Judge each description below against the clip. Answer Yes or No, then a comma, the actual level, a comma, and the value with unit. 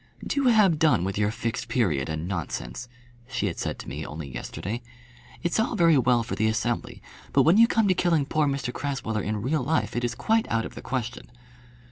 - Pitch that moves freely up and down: Yes, wide, 6.9 semitones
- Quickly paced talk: Yes, fast, 210 wpm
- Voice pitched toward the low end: Yes, low, 125 Hz